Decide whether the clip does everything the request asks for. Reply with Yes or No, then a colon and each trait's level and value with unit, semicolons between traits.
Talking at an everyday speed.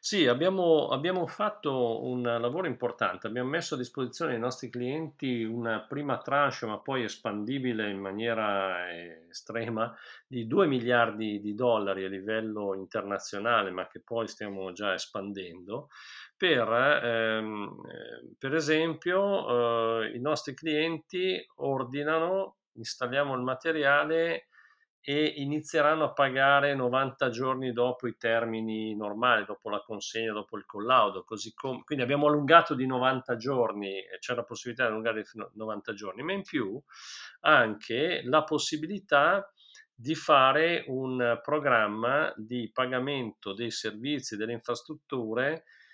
Yes: average, 130 wpm